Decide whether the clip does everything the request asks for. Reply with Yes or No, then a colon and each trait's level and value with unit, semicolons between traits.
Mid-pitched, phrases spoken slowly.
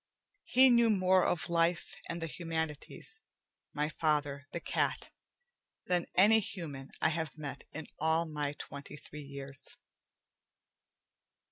Yes: medium, 160 Hz; slow, 125 wpm